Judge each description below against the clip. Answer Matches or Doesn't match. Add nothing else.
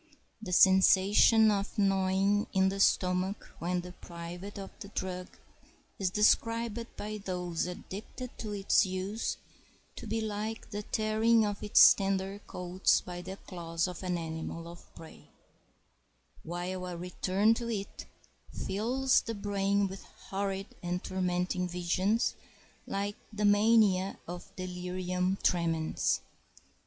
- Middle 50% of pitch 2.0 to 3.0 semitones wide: Matches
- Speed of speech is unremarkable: Doesn't match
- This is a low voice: Doesn't match